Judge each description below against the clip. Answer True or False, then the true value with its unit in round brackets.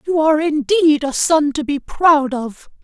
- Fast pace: False (190 wpm)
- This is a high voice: True (285 Hz)